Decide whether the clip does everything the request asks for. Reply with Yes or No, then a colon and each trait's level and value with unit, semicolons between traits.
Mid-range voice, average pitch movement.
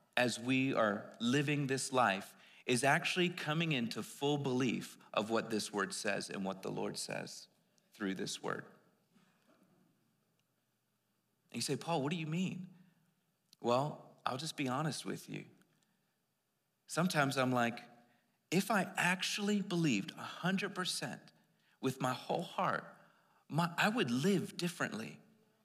No: medium, 145 Hz; wide, 6.3 semitones